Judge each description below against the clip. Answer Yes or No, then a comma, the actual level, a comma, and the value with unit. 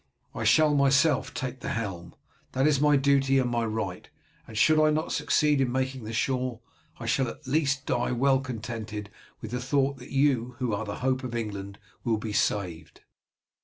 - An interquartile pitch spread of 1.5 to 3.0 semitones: No, average, 3.7 semitones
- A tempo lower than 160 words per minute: No, average, 190 wpm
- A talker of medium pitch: No, low, 130 Hz